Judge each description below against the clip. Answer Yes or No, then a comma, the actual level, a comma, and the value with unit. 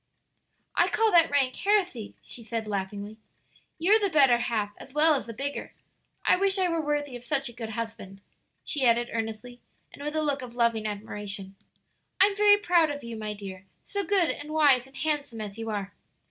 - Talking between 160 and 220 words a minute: Yes, average, 195 wpm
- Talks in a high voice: Yes, very high, 255 Hz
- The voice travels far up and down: Yes, wide, 6.1 semitones